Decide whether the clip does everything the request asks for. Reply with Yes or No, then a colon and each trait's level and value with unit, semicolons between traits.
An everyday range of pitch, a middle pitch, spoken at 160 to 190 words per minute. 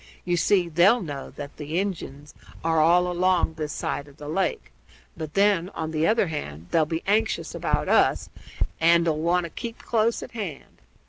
Yes: average, 3.4 semitones; medium, 170 Hz; average, 185 wpm